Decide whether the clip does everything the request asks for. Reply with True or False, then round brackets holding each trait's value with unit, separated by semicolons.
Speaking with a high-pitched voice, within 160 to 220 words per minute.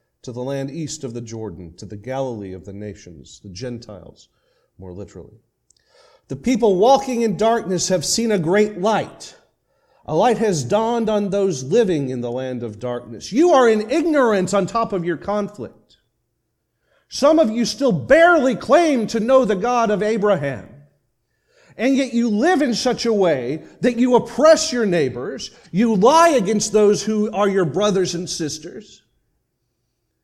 True (205 Hz; 165 wpm)